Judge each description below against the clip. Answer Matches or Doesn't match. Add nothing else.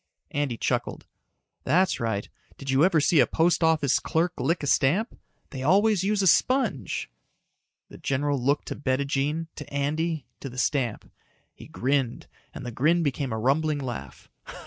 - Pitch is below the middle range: Doesn't match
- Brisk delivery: Doesn't match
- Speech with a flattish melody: Doesn't match